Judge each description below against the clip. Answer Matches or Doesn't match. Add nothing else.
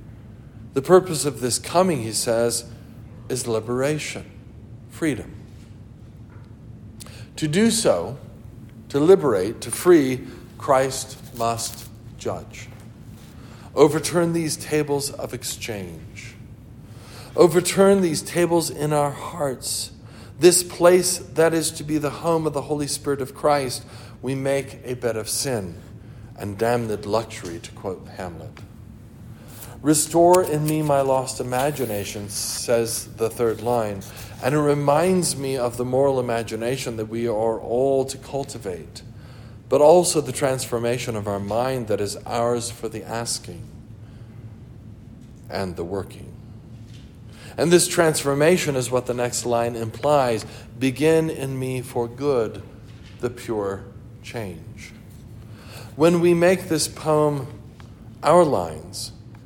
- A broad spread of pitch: Doesn't match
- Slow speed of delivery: Matches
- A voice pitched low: Matches